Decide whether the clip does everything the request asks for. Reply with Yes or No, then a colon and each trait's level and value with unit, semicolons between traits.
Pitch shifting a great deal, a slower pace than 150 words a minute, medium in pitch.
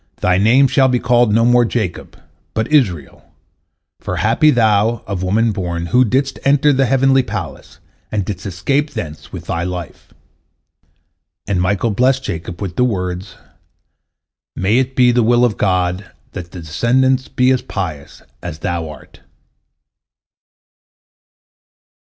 No: wide, 5.8 semitones; average, 140 wpm; low, 110 Hz